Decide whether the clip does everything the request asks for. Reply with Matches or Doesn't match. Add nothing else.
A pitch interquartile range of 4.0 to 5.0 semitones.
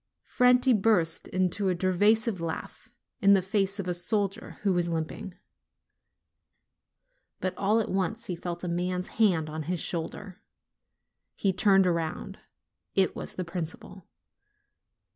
Doesn't match